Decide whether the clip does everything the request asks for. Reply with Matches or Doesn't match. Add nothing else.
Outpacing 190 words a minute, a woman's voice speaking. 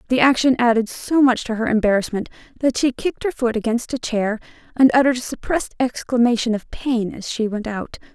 Matches